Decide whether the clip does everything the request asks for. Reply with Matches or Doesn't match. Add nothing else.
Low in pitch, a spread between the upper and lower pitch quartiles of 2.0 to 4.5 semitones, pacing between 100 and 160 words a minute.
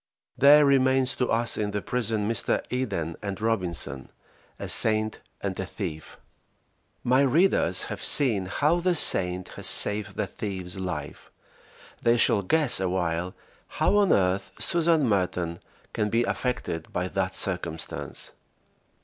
Doesn't match